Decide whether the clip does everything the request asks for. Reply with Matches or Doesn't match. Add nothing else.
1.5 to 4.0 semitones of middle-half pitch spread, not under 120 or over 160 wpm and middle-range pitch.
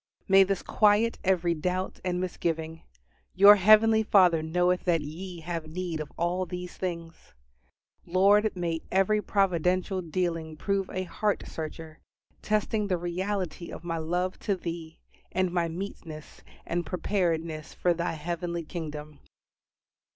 Matches